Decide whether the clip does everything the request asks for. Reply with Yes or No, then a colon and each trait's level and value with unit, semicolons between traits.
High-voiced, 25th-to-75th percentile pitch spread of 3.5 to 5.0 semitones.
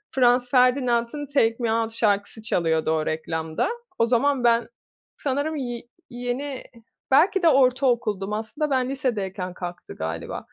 Yes: high, 240 Hz; average, 4.6 semitones